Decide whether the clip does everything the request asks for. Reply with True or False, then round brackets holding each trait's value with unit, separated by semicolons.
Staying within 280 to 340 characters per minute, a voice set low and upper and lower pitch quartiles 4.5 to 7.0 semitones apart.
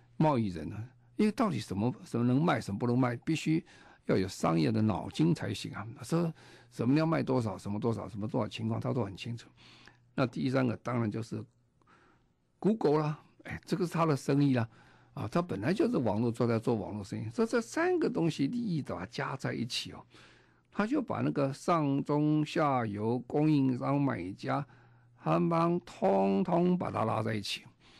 True (285 characters per minute; 125 Hz; 5.5 semitones)